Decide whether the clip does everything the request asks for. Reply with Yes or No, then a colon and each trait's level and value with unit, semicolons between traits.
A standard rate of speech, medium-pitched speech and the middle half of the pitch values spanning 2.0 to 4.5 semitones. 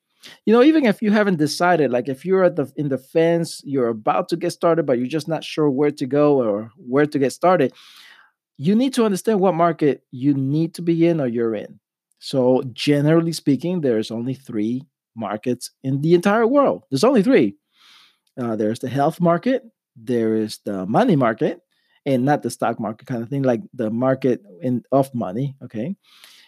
No: average, 195 wpm; medium, 145 Hz; average, 5.2 semitones